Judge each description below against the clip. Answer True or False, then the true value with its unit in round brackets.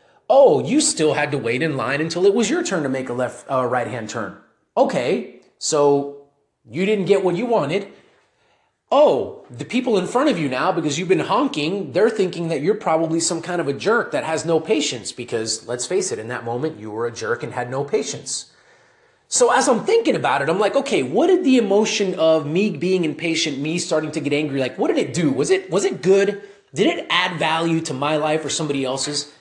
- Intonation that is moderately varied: False (5.8 semitones)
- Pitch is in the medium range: True (160 Hz)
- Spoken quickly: True (230 wpm)